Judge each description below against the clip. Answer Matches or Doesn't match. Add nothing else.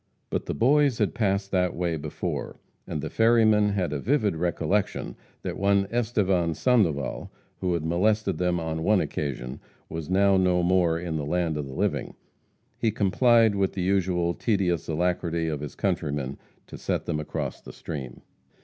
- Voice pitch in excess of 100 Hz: Doesn't match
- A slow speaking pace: Doesn't match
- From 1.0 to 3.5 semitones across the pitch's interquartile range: Doesn't match